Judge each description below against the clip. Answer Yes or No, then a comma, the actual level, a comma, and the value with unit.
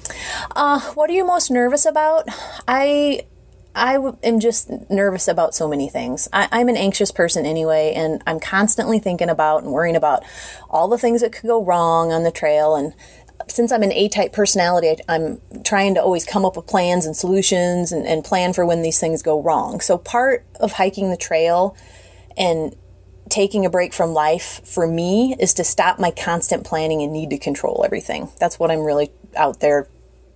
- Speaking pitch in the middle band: Yes, medium, 180 Hz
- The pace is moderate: Yes, average, 195 wpm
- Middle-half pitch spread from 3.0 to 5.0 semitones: No, wide, 5.6 semitones